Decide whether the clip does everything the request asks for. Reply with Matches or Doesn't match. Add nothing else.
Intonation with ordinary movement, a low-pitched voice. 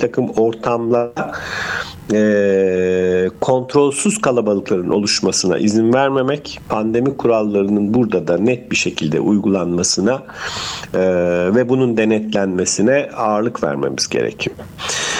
Matches